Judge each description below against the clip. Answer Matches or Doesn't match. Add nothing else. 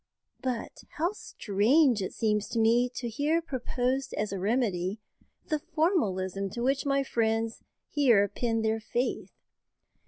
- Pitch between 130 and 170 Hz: Doesn't match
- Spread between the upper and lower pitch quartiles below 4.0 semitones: Doesn't match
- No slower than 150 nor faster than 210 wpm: Doesn't match